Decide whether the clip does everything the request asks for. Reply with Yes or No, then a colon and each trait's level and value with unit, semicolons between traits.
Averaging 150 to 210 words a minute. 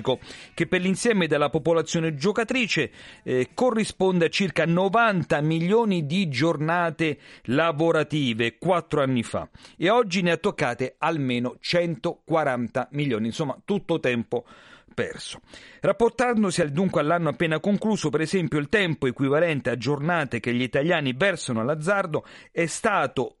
No: average, 130 wpm